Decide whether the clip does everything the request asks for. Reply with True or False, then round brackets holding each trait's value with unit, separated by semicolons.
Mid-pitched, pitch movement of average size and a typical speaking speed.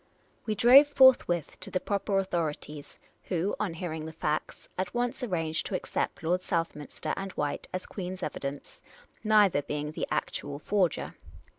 True (180 Hz; 4.5 semitones; 165 wpm)